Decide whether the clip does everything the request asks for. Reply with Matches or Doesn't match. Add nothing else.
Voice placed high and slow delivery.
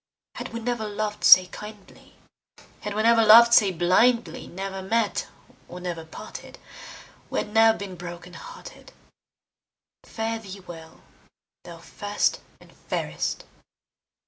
Matches